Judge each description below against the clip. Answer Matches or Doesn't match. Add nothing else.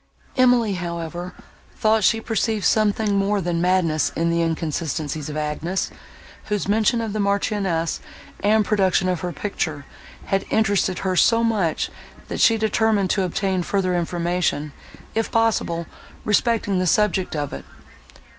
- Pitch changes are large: Doesn't match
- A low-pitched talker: Doesn't match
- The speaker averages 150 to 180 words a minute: Doesn't match